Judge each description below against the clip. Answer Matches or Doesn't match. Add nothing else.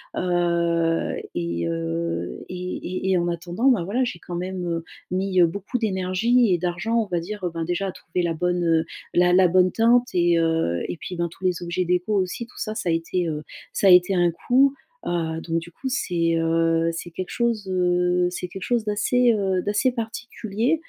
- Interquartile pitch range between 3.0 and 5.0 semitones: Matches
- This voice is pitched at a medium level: Matches